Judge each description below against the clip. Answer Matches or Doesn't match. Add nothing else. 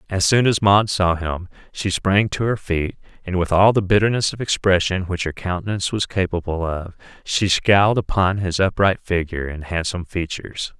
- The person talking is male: Matches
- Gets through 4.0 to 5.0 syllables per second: Doesn't match